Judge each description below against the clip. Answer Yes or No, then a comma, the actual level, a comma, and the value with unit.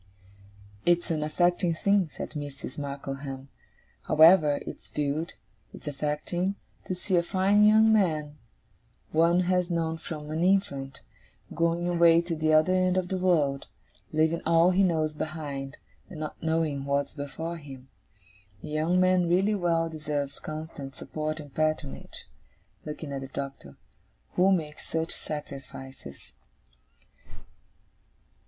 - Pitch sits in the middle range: Yes, medium, 160 Hz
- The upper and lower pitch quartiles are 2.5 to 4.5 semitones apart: Yes, average, 3.2 semitones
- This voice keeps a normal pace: No, slow, 130 wpm